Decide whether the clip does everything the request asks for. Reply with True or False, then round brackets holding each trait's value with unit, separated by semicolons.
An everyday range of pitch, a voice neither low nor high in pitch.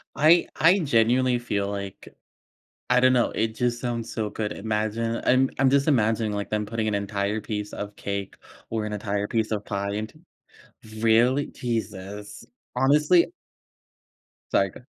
False (3.3 semitones; 110 Hz)